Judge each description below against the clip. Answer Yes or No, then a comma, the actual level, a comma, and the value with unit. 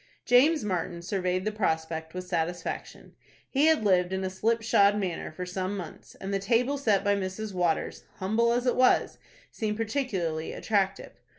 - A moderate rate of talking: Yes, average, 170 wpm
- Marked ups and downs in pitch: No, average, 3.8 semitones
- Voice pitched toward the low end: No, high, 195 Hz